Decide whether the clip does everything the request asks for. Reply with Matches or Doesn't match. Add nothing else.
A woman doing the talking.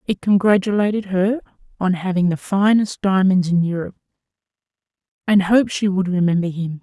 Matches